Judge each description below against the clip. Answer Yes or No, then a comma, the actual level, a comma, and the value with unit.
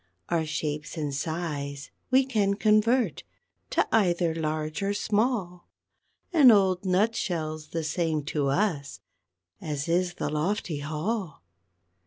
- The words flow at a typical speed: No, slow, 130 wpm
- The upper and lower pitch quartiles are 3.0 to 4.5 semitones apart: No, average, 5.0 semitones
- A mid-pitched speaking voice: Yes, medium, 170 Hz